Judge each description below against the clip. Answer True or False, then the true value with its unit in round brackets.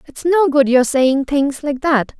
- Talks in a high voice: True (280 Hz)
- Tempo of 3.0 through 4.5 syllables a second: True (4.0 syllables/s)